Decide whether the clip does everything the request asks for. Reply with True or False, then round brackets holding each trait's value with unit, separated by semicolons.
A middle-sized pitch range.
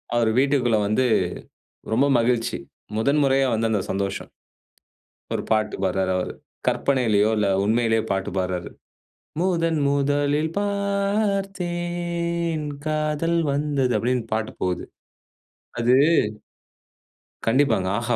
False (7.0 semitones)